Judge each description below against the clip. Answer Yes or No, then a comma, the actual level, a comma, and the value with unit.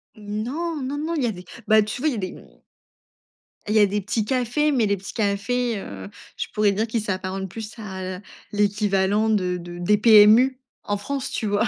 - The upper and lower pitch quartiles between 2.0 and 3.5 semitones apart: Yes, average, 3.2 semitones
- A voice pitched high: Yes, high, 210 Hz